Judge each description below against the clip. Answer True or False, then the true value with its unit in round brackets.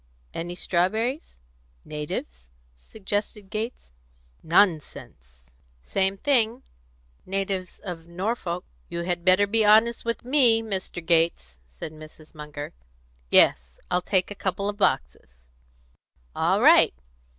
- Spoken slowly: True (110 wpm)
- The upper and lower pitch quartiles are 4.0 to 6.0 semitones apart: True (5.2 semitones)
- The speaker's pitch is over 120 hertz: True (185 Hz)